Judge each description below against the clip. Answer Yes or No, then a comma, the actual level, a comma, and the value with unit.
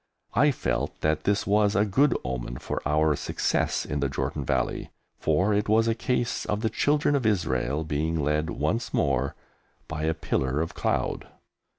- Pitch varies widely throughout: Yes, wide, 6.5 semitones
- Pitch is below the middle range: Yes, very low, 80 Hz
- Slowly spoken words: No, average, 175 wpm